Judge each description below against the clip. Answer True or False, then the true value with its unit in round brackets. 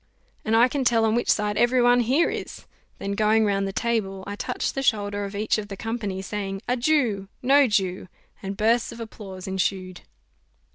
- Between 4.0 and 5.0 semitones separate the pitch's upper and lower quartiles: False (3.3 semitones)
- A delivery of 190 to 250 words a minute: True (195 wpm)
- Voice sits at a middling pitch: False (215 Hz)